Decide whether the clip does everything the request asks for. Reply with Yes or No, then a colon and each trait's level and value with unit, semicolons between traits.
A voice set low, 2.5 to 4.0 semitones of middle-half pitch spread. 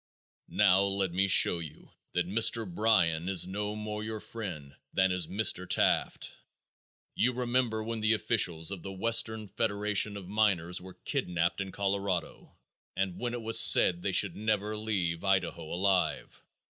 Yes: low, 100 Hz; average, 3.3 semitones